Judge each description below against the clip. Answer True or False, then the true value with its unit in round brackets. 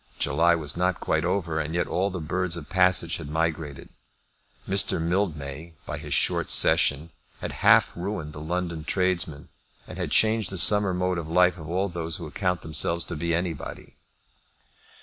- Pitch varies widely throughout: False (2.5 semitones)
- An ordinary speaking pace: True (170 wpm)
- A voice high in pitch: False (85 Hz)